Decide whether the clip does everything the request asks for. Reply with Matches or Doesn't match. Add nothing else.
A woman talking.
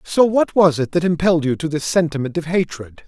Doesn't match